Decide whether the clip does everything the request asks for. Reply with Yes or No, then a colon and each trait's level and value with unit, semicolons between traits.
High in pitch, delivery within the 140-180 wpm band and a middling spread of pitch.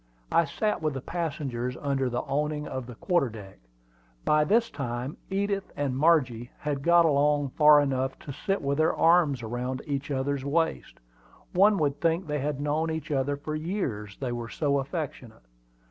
No: medium, 145 Hz; average, 175 wpm; average, 3.4 semitones